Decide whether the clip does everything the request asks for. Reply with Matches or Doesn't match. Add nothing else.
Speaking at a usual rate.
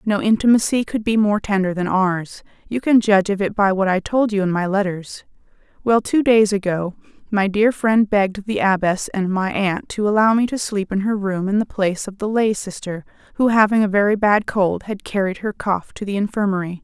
Doesn't match